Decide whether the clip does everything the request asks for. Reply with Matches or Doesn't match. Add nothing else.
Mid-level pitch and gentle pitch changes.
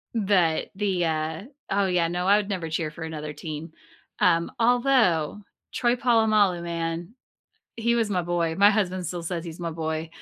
Doesn't match